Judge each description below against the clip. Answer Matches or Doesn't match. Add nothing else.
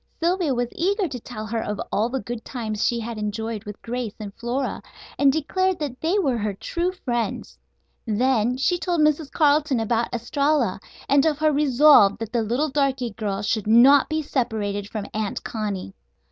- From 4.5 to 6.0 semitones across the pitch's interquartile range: Matches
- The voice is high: Matches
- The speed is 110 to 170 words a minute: Doesn't match